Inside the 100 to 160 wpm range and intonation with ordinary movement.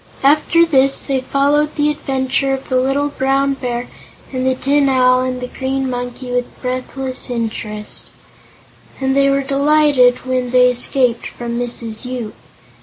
No: average, 145 wpm; narrow, 1.8 semitones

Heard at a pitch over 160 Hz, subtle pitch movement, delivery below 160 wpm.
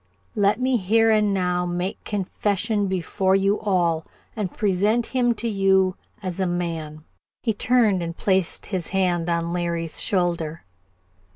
No: high, 190 Hz; average, 3.0 semitones; average, 150 wpm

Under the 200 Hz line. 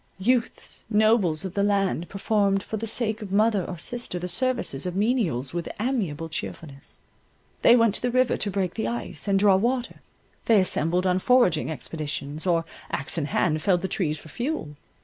Yes: high, 190 Hz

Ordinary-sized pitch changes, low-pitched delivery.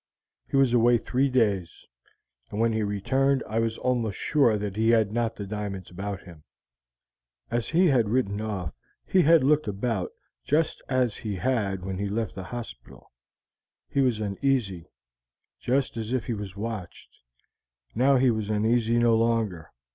Yes: average, 3.7 semitones; low, 115 Hz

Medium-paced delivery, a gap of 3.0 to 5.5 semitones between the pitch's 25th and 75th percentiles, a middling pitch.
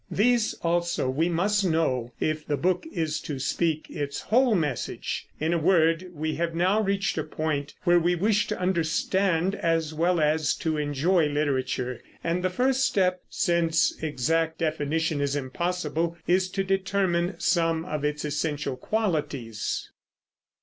Yes: average, 150 wpm; average, 3.4 semitones; medium, 165 Hz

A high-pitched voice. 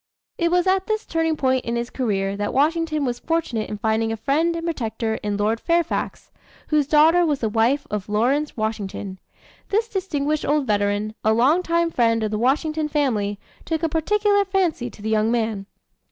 Yes: very high, 270 Hz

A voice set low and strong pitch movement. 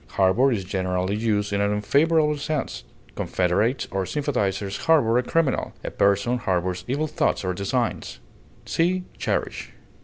Yes: low, 105 Hz; wide, 6.7 semitones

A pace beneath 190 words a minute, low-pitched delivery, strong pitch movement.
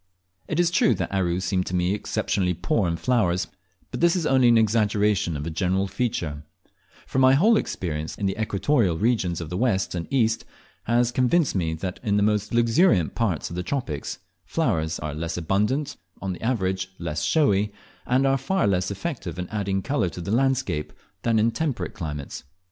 No: average, 195 wpm; low, 100 Hz; wide, 6.0 semitones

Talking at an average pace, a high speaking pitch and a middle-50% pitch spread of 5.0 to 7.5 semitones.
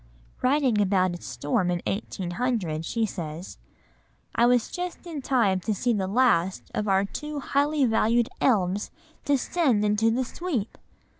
Yes: average, 145 wpm; high, 225 Hz; wide, 5.4 semitones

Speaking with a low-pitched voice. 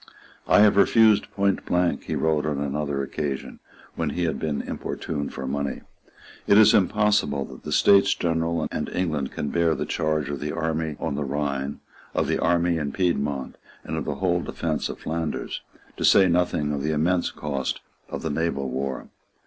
Yes: very low, 80 Hz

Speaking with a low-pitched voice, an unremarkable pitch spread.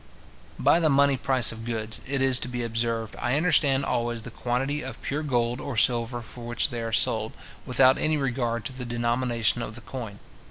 No: low, 120 Hz; narrow, 2.3 semitones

